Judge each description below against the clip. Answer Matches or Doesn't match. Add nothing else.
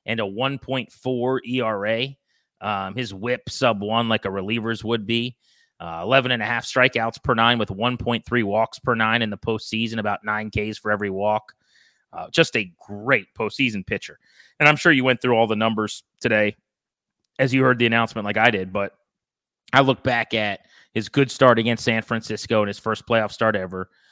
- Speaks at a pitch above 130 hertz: Doesn't match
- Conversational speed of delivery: Matches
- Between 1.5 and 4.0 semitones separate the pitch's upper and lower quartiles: Matches